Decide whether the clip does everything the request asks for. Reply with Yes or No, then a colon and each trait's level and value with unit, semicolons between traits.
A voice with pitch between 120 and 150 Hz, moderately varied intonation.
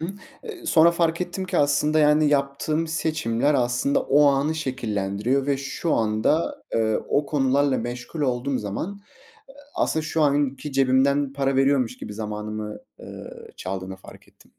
Yes: medium, 140 Hz; average, 4.0 semitones